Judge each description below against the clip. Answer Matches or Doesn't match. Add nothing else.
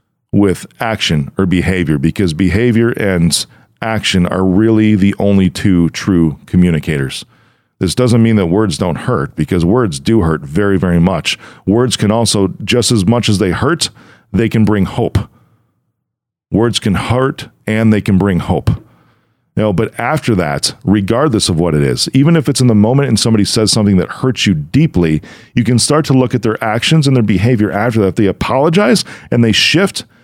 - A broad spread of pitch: Doesn't match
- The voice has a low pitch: Matches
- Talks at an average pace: Matches